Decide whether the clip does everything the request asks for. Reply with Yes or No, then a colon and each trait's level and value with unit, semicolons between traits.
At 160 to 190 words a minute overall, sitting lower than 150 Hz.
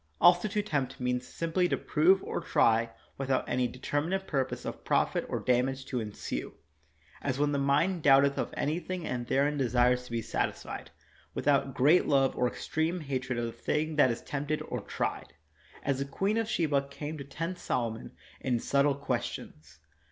Yes: average, 175 wpm; medium, 140 Hz